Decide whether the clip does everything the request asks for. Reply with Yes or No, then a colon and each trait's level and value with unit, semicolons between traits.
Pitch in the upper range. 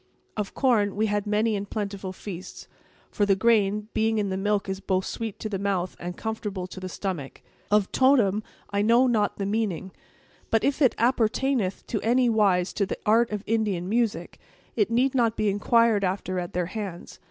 Yes: high, 210 Hz